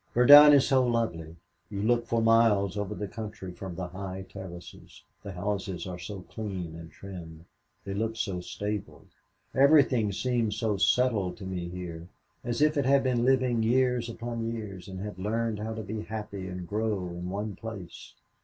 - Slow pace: No, average, 175 wpm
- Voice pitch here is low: Yes, low, 105 Hz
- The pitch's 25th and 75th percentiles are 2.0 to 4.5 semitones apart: Yes, average, 3.8 semitones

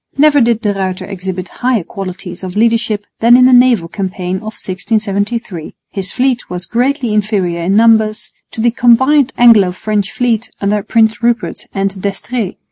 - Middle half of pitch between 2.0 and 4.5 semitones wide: Yes, average, 3.7 semitones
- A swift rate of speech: No, average, 160 wpm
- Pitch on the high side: Yes, high, 215 Hz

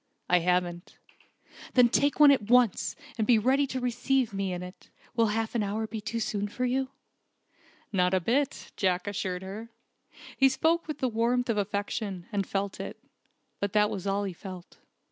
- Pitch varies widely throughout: No, average, 4.3 semitones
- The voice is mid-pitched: No, high, 215 Hz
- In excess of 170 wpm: Yes, average, 185 wpm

